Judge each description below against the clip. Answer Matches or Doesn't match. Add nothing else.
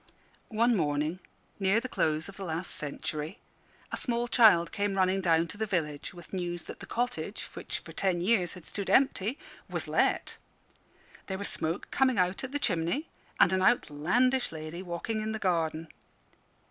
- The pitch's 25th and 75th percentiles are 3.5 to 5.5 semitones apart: Matches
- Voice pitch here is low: Doesn't match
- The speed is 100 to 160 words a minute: Doesn't match